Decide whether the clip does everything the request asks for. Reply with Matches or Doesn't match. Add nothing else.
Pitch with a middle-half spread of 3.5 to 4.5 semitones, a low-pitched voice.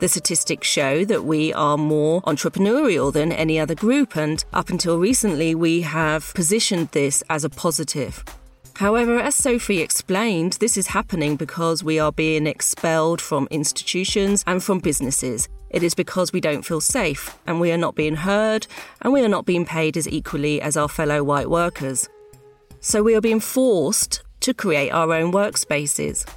Doesn't match